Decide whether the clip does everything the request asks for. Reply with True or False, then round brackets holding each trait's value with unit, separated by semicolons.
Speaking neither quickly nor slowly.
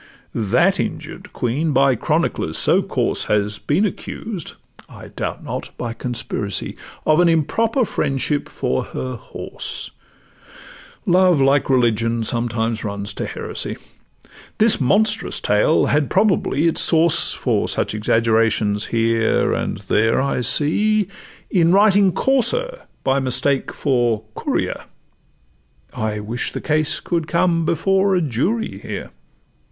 False (125 wpm)